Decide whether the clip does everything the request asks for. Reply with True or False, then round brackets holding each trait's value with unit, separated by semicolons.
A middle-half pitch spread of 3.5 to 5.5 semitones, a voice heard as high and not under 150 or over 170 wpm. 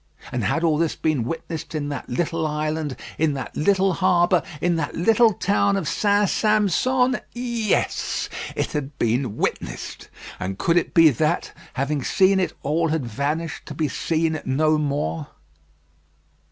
False (4.5 semitones; 160 Hz; 155 wpm)